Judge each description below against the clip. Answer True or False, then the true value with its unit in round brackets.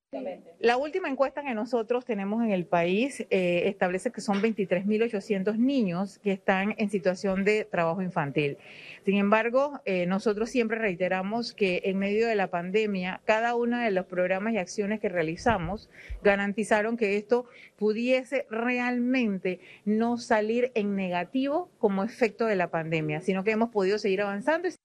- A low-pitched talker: False (210 Hz)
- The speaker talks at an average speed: True (155 wpm)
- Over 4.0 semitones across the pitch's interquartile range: False (3.5 semitones)